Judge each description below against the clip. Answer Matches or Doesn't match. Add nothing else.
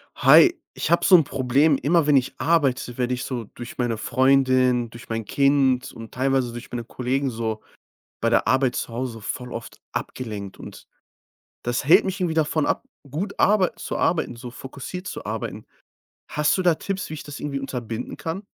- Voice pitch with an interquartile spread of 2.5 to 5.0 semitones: Matches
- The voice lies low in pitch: Matches